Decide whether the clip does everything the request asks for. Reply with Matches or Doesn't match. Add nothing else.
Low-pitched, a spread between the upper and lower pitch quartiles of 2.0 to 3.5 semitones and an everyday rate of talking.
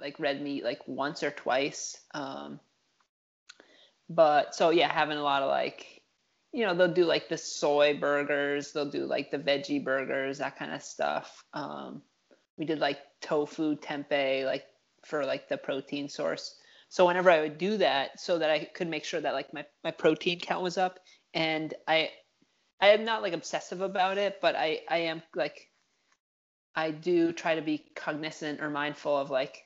Doesn't match